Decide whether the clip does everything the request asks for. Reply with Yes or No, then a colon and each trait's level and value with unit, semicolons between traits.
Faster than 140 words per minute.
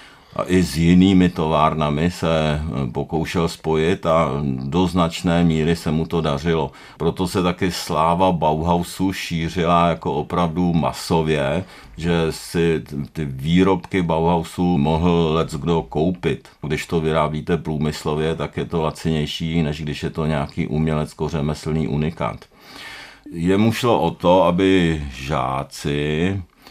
No: average, 125 wpm